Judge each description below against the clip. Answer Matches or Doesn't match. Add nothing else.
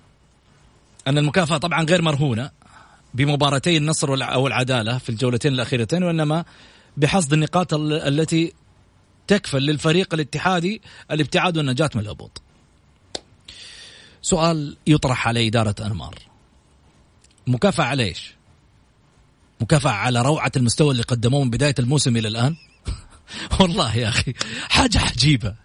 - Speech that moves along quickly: Doesn't match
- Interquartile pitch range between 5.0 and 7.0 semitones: Matches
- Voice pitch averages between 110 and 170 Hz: Matches